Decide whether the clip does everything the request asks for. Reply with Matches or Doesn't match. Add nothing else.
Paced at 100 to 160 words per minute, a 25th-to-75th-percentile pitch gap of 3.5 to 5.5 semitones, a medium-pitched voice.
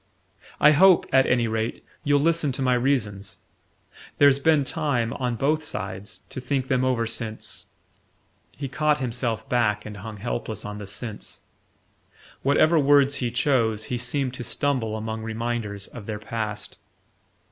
Doesn't match